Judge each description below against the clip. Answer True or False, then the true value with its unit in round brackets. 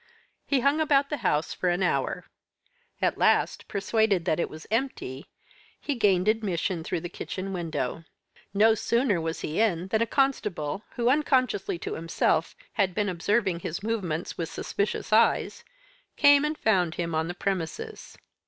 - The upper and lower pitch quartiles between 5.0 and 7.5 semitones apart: True (5.3 semitones)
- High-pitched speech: True (195 Hz)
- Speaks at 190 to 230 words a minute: False (160 wpm)